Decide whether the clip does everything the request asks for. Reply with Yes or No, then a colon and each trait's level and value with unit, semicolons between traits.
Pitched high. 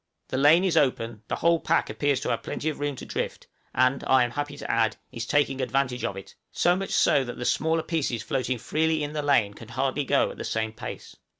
No: low, 135 Hz